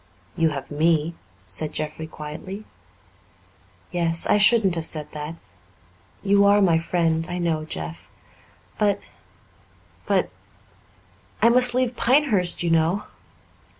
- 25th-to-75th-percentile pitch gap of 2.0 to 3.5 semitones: No, average, 4.3 semitones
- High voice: No, medium, 170 Hz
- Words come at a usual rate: No, slow, 115 wpm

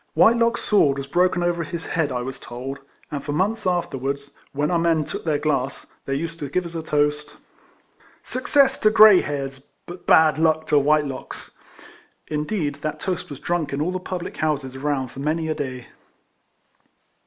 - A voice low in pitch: No, medium, 150 Hz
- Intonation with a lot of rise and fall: No, average, 3.8 semitones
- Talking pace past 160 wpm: Yes, average, 190 wpm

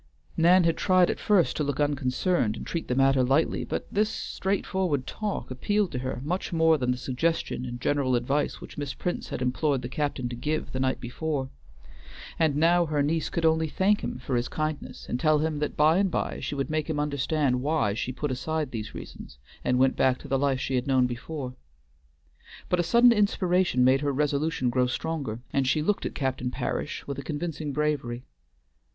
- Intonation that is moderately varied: Yes, average, 4.0 semitones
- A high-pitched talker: No, medium, 145 Hz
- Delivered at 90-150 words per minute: No, fast, 205 wpm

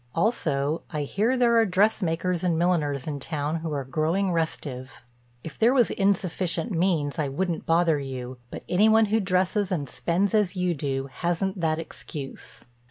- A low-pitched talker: No, medium, 170 Hz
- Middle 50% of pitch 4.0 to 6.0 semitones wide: Yes, average, 4.7 semitones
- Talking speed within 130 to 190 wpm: Yes, average, 165 wpm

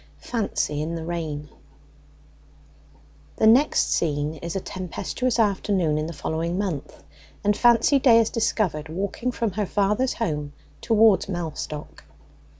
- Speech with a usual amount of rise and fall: No, wide, 5.9 semitones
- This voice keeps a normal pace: No, slow, 130 wpm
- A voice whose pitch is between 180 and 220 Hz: Yes, medium, 185 Hz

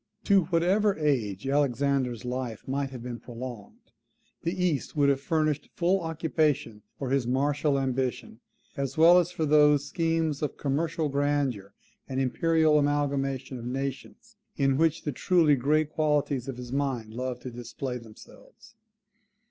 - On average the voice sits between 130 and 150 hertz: Yes, medium, 140 Hz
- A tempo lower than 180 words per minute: Yes, average, 145 wpm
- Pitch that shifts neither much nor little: Yes, average, 3.4 semitones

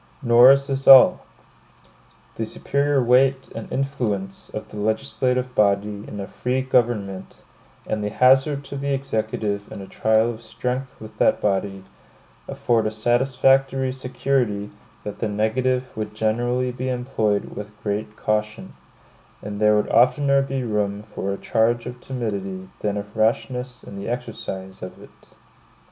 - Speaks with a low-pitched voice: Yes, low, 115 Hz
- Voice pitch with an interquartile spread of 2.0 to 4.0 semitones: Yes, average, 3.6 semitones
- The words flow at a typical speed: Yes, average, 150 wpm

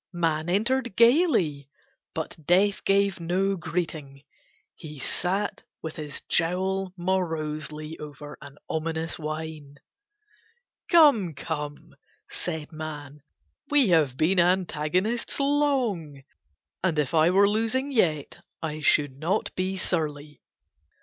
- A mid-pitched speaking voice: Yes, medium, 165 Hz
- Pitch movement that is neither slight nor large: Yes, average, 4.3 semitones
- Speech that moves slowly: Yes, slow, 110 wpm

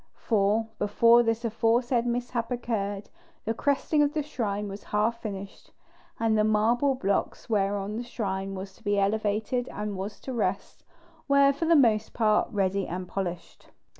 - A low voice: No, high, 220 Hz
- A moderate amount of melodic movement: Yes, average, 3.1 semitones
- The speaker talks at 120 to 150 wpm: No, average, 160 wpm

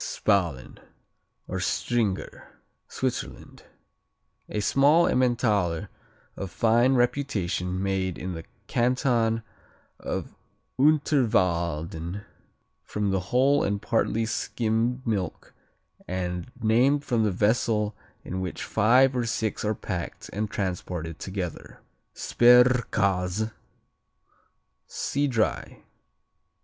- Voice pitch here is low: Yes, low, 110 Hz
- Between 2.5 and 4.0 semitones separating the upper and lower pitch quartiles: No, average, 4.8 semitones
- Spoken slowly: Yes, slow, 90 wpm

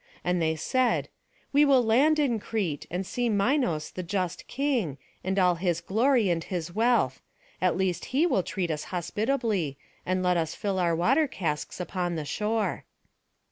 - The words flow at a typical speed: Yes, average, 170 wpm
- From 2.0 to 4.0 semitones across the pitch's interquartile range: No, wide, 5.6 semitones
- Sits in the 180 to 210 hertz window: Yes, high, 190 Hz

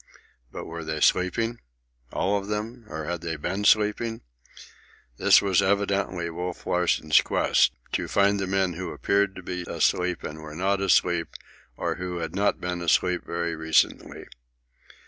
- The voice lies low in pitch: Yes, very low, 90 Hz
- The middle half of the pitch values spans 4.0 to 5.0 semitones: No, average, 2.9 semitones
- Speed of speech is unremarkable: Yes, average, 155 wpm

